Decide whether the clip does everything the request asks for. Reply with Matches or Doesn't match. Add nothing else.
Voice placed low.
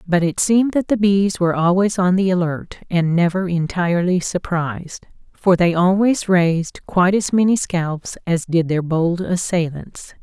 Doesn't match